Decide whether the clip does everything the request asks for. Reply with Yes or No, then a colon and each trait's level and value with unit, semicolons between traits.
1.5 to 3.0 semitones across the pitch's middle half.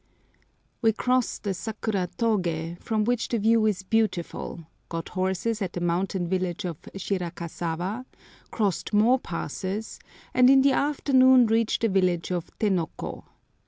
No: average, 4.4 semitones